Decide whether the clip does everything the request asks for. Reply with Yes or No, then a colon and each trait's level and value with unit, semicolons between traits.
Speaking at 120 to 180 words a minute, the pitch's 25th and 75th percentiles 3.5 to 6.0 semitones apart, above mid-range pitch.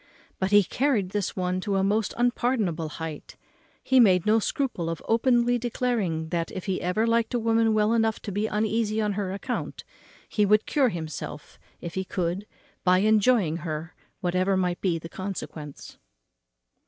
Yes: average, 165 wpm; average, 4.1 semitones; high, 200 Hz